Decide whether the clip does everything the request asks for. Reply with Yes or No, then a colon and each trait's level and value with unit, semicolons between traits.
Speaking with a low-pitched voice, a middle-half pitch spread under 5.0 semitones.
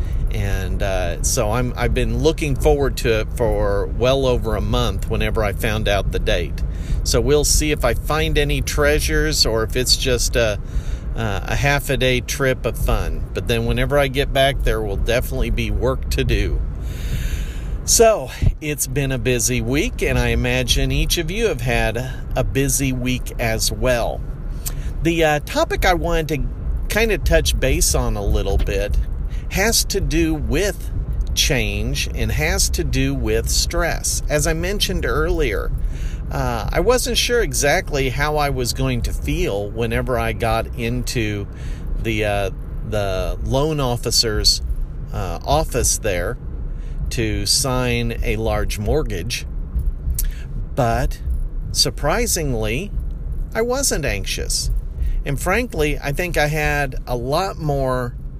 No: low, 125 Hz; wide, 5.4 semitones